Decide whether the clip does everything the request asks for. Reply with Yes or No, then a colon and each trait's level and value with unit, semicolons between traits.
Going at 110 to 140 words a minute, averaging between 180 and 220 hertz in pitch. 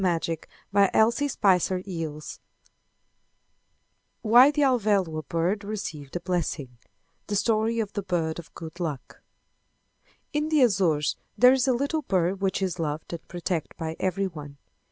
Yes: slow, 135 wpm; medium, 185 Hz